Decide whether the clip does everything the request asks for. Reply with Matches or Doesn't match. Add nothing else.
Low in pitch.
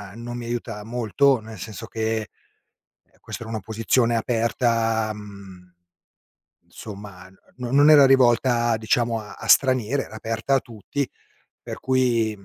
Matches